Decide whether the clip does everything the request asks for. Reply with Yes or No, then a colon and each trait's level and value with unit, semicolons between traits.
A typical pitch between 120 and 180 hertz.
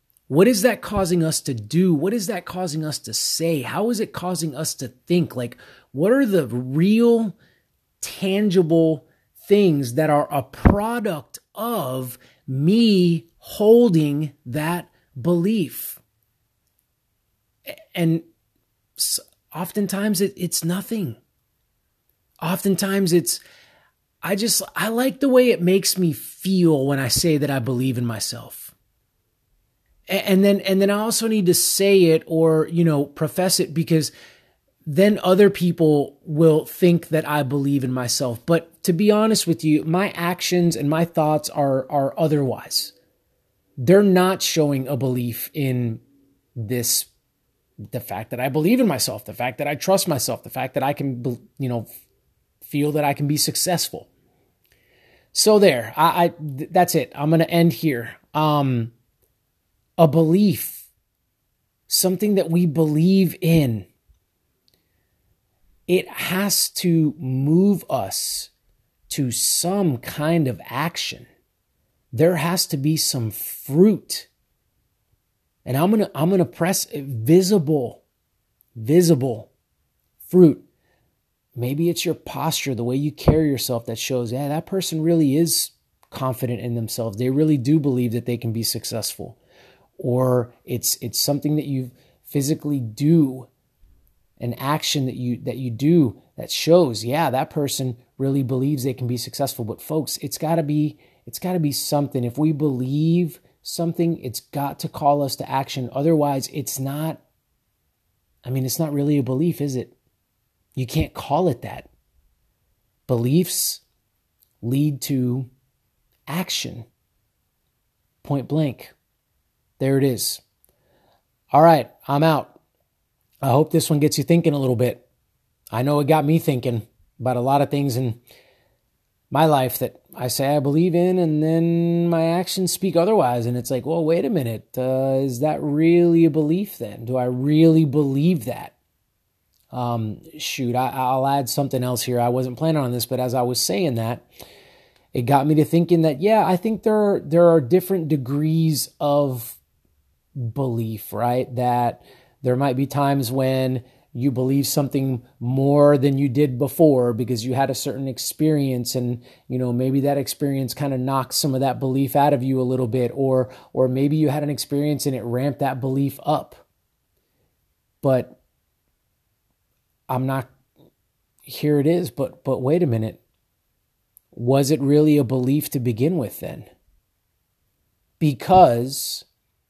Yes: medium, 140 Hz